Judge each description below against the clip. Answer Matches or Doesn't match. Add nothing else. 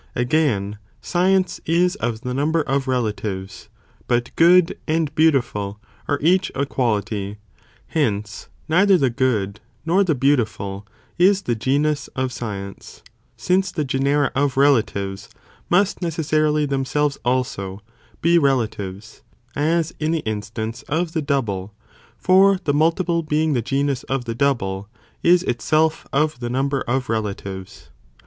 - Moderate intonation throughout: Doesn't match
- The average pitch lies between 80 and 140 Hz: Matches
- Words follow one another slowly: Matches